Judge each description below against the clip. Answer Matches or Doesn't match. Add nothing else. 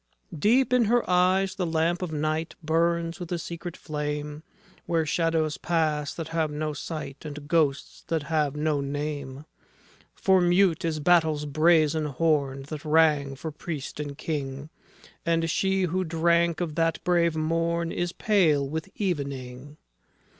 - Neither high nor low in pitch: Matches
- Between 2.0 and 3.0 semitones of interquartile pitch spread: Matches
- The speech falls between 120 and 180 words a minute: Matches